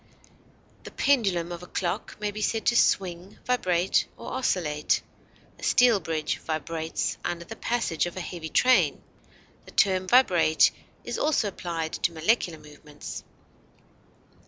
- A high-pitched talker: No, medium, 180 Hz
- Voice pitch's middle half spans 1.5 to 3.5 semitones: No, average, 4.7 semitones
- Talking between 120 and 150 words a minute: Yes, slow, 135 wpm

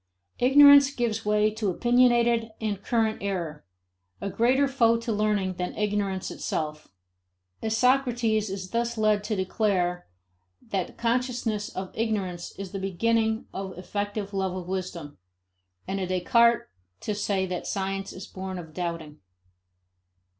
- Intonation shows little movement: No, average, 3.6 semitones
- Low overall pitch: No, high, 205 Hz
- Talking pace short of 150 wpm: Yes, slow, 135 wpm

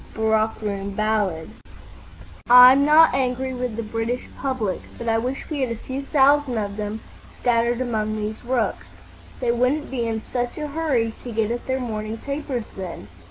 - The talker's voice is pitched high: Yes, high, 235 Hz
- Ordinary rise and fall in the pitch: Yes, average, 3.2 semitones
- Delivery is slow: No, average, 170 wpm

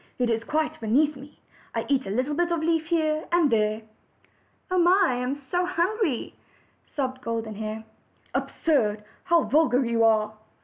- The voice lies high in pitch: Yes, very high, 275 Hz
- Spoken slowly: No, average, 160 wpm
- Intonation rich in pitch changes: Yes, wide, 6.3 semitones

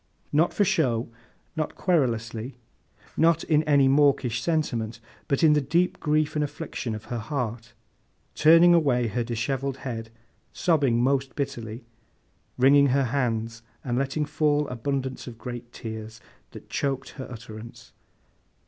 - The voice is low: Yes, low, 130 Hz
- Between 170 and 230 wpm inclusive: No, slow, 135 wpm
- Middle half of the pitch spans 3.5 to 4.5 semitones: Yes, average, 4.1 semitones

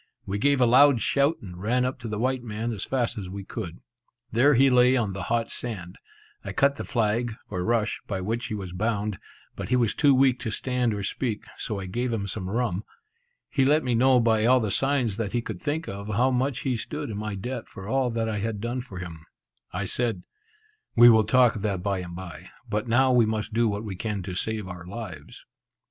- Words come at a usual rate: No, fast, 230 wpm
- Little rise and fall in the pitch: No, average, 3.8 semitones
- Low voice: Yes, low, 115 Hz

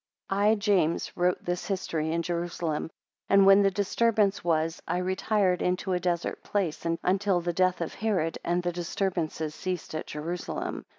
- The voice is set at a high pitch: No, medium, 180 Hz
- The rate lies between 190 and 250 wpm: No, average, 160 wpm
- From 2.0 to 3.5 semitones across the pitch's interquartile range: Yes, narrow, 2.6 semitones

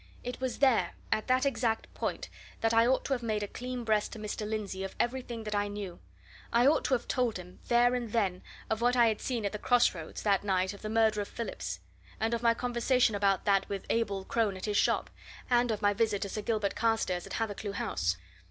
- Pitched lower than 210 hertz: No, high, 220 Hz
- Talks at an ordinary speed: No, fast, 235 wpm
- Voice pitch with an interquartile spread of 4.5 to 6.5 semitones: No, average, 2.9 semitones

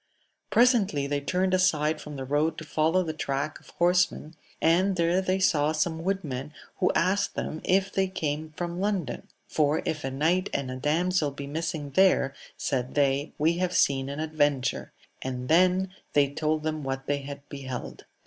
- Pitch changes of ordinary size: Yes, average, 4.1 semitones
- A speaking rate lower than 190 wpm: Yes, average, 175 wpm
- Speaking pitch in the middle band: Yes, medium, 155 Hz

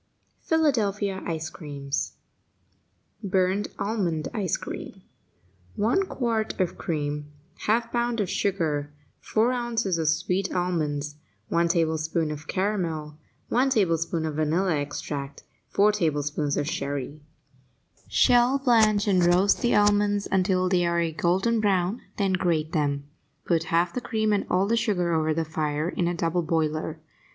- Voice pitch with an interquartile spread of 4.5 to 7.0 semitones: Yes, average, 4.8 semitones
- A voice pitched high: No, medium, 175 Hz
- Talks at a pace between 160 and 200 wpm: No, average, 140 wpm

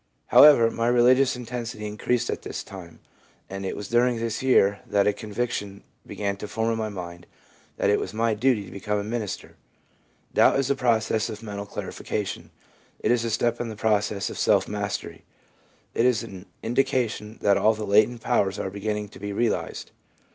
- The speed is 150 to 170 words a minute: No, average, 190 wpm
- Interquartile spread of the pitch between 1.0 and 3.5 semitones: Yes, average, 2.8 semitones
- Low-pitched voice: Yes, low, 110 Hz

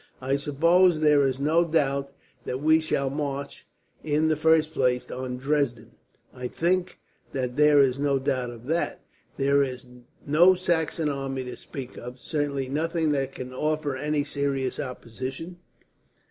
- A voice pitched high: No, medium, 140 Hz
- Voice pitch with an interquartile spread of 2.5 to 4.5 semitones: Yes, average, 2.8 semitones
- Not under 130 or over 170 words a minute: Yes, average, 150 wpm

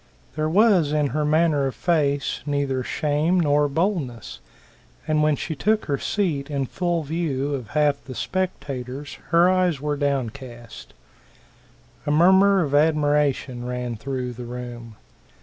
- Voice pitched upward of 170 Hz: No, medium, 145 Hz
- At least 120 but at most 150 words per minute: Yes, average, 140 wpm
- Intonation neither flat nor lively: Yes, average, 3.5 semitones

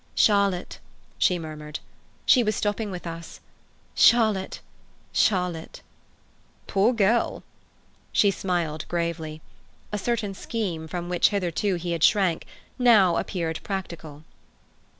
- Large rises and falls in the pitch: No, average, 3.7 semitones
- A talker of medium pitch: Yes, medium, 180 Hz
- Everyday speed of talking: No, slow, 105 wpm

